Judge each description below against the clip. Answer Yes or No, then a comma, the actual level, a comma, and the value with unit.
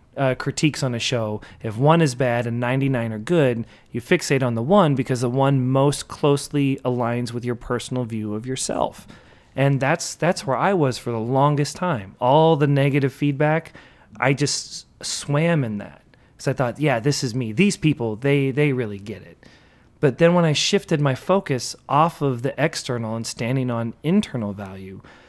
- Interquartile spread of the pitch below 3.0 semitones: No, average, 3.6 semitones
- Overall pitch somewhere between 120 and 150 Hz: Yes, low, 135 Hz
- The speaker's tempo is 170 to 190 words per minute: Yes, average, 180 wpm